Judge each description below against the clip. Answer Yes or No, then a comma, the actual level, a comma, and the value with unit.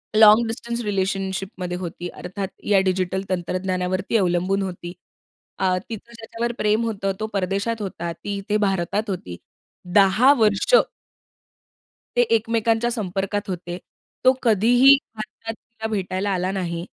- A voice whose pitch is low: No, high, 195 Hz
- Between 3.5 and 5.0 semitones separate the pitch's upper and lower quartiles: No, average, 3.1 semitones